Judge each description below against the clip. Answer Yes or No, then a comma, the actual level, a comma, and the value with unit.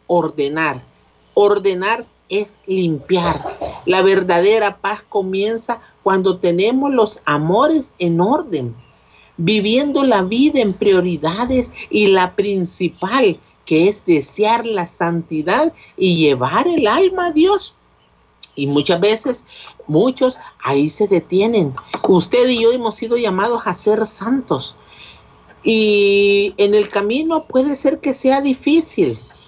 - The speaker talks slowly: Yes, slow, 120 wpm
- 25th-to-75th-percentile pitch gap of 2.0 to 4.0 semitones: No, wide, 5.6 semitones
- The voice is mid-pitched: No, high, 200 Hz